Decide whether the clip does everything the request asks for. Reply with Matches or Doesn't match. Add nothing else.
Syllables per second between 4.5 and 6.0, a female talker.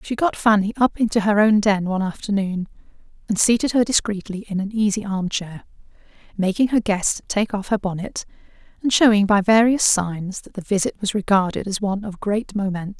Matches